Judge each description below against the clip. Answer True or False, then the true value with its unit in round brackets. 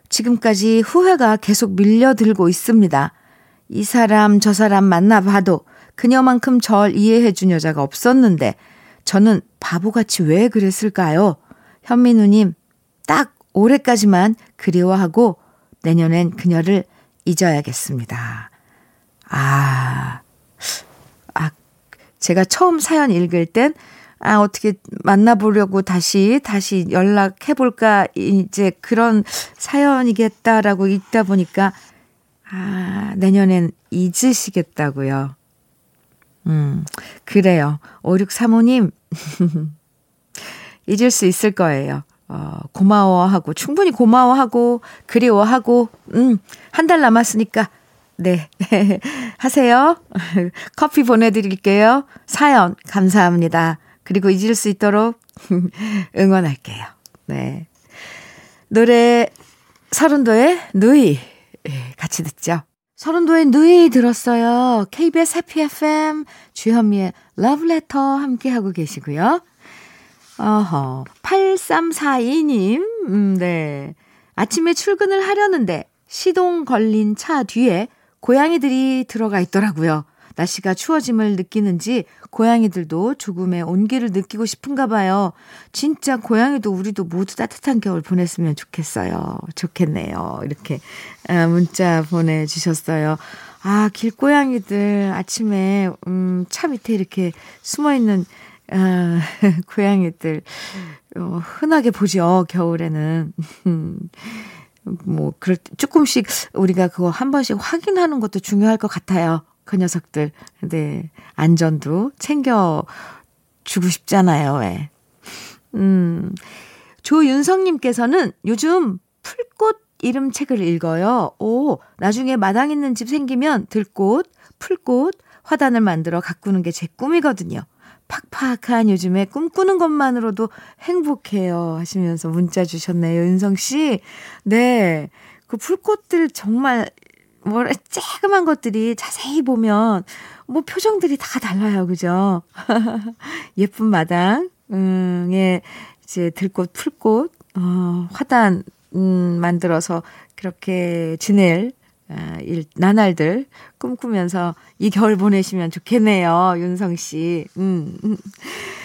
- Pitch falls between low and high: False (205 Hz)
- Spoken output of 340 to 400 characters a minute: False (225 characters per minute)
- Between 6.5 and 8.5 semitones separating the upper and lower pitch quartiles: False (5.5 semitones)